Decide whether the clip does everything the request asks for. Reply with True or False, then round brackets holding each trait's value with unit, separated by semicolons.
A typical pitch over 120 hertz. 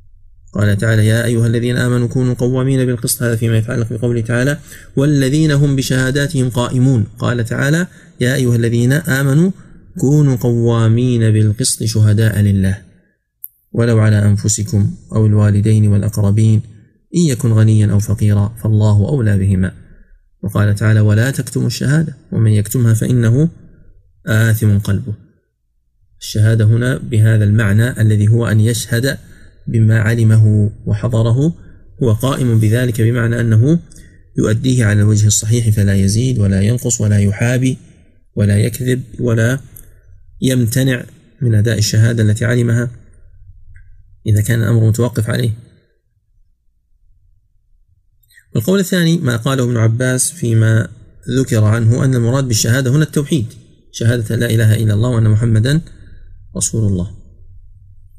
False (115 Hz)